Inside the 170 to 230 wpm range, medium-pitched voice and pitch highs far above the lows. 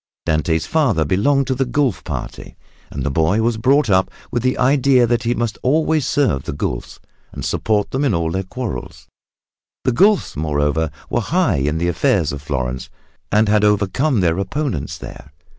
No: average, 175 wpm; low, 105 Hz; wide, 8.4 semitones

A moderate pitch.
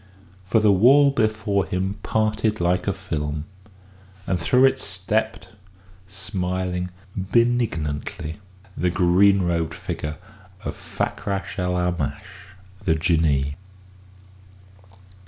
No: very low, 95 Hz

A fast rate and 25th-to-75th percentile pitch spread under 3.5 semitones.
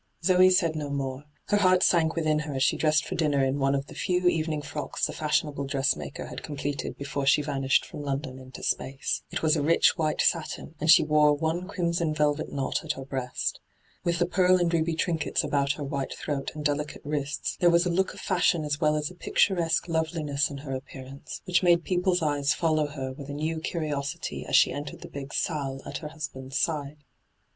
Yes: fast, 210 wpm; average, 2.8 semitones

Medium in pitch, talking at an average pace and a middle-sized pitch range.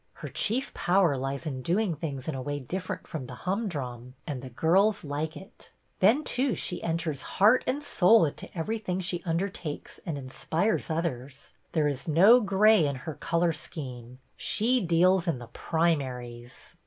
No: medium, 165 Hz; average, 160 wpm; wide, 5.8 semitones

